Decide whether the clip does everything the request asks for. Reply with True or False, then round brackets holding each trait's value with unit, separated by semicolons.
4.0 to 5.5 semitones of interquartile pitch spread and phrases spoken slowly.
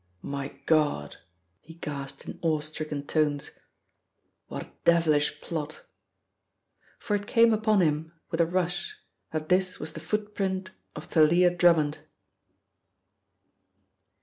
False (3.5 semitones; 120 wpm)